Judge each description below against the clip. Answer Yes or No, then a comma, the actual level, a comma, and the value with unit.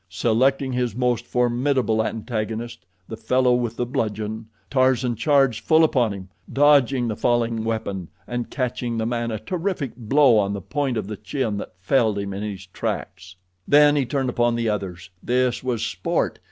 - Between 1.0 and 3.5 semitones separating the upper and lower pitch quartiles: Yes, average, 3.2 semitones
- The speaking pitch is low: Yes, low, 120 Hz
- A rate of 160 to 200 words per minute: Yes, average, 170 wpm